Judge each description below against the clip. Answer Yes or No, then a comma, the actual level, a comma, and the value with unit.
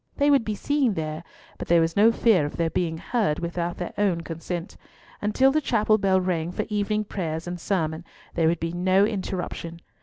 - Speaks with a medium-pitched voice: Yes, medium, 180 Hz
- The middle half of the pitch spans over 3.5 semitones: Yes, average, 4.0 semitones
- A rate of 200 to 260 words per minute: Yes, fast, 205 wpm